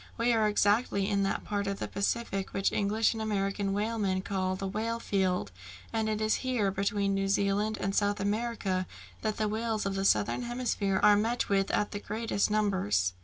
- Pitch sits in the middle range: No, high, 205 Hz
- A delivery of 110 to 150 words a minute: No, average, 190 wpm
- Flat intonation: Yes, narrow, 1.8 semitones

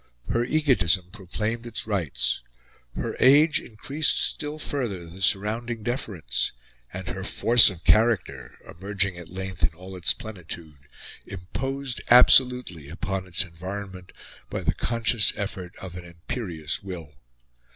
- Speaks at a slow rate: Yes, slow, 130 wpm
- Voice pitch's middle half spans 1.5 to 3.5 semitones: No, average, 5.3 semitones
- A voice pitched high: No, very low, 95 Hz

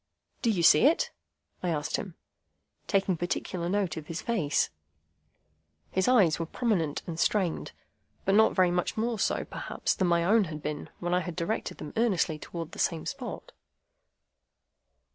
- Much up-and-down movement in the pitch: No, average, 4.2 semitones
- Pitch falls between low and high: Yes, medium, 180 Hz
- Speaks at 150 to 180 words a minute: Yes, average, 160 wpm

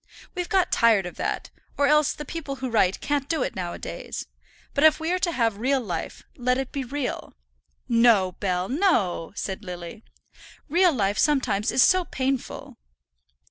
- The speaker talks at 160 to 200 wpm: Yes, average, 180 wpm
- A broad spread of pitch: Yes, wide, 6.7 semitones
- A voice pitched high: Yes, very high, 260 Hz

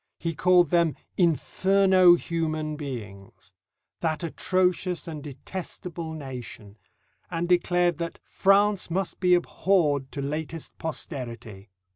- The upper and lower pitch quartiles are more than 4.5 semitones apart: No, average, 3.8 semitones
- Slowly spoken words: Yes, slow, 105 wpm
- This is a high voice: No, medium, 165 Hz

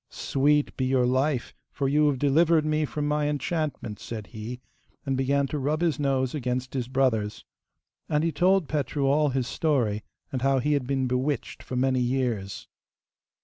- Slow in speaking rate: No, average, 175 wpm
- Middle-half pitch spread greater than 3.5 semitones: No, average, 2.8 semitones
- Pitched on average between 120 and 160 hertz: Yes, low, 135 Hz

